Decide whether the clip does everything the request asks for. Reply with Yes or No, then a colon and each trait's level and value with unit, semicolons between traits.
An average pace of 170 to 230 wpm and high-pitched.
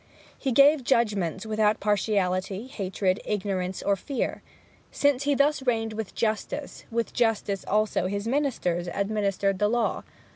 No: slow, 135 wpm; high, 215 Hz